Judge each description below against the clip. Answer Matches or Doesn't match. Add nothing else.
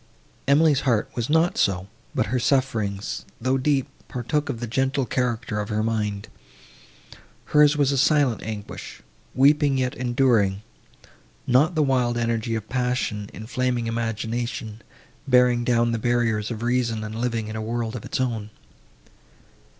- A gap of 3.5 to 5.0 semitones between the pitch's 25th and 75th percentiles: Doesn't match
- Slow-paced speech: Doesn't match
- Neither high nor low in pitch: Doesn't match